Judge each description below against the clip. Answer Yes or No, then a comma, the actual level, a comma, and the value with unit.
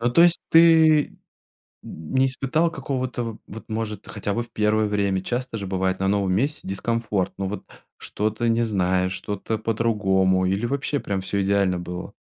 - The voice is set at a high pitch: No, low, 105 Hz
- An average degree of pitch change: Yes, average, 4.0 semitones